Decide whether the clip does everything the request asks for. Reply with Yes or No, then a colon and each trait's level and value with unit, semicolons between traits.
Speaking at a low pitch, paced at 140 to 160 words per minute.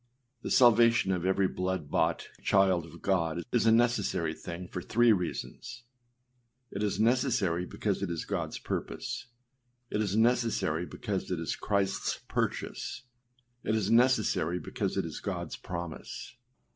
Yes: low, 100 Hz; average, 145 wpm